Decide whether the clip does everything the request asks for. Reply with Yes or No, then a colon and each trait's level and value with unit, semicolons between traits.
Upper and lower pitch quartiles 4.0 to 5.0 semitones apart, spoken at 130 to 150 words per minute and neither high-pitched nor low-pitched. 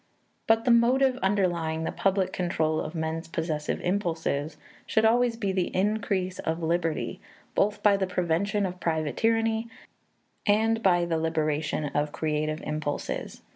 Yes: average, 4.6 semitones; average, 140 wpm; medium, 180 Hz